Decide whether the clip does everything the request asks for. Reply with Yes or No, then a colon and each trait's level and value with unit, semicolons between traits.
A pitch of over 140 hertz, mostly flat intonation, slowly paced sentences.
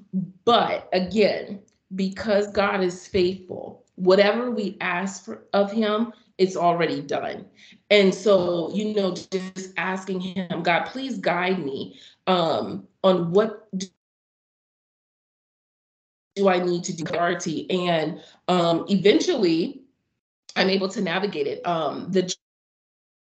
Yes: high, 190 Hz; narrow, 2.3 semitones; slow, 115 wpm